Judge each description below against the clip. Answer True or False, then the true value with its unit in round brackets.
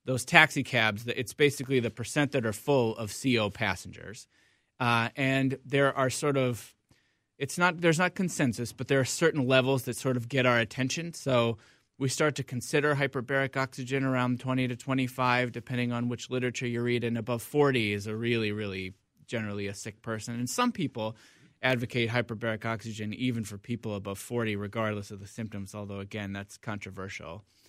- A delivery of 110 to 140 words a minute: False (180 wpm)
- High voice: False (120 Hz)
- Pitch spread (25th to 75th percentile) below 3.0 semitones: False (3.5 semitones)